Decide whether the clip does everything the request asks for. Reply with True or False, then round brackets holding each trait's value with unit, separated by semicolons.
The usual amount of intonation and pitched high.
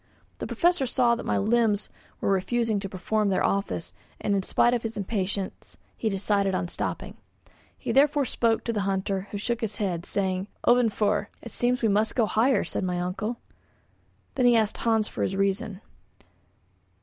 True (3.3 semitones; 210 Hz)